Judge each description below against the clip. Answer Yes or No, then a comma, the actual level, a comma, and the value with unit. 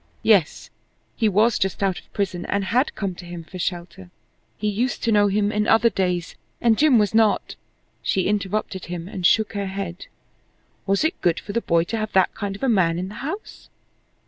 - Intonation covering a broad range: No, average, 3.1 semitones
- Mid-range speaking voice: No, high, 200 Hz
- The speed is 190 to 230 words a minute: Yes, fast, 205 wpm